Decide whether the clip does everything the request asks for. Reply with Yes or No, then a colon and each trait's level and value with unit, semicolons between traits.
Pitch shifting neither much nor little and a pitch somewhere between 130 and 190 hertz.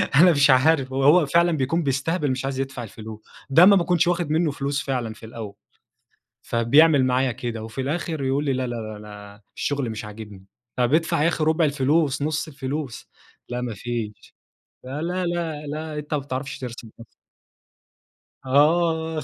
Yes: average, 4.5 semitones; medium, 140 Hz